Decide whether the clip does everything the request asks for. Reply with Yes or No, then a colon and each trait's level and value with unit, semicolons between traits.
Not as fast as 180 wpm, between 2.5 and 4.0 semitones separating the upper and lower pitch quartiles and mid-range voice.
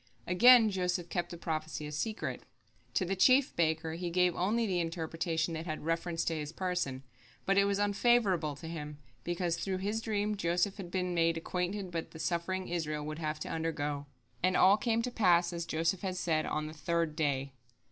No: average, 195 wpm; average, 3.0 semitones; medium, 175 Hz